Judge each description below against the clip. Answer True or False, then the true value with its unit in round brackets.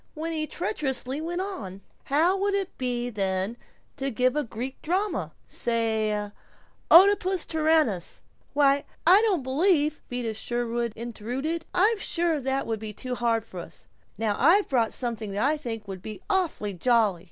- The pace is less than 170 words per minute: True (160 wpm)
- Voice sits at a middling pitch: False (255 Hz)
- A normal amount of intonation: False (6.5 semitones)